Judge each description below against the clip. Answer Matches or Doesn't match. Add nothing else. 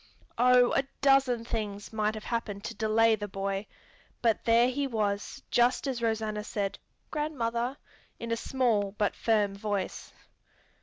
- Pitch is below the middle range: Doesn't match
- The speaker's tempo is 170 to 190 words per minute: Doesn't match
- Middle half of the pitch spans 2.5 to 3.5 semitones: Matches